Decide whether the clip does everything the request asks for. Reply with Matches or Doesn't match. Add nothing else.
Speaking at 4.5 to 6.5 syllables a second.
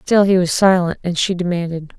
Matches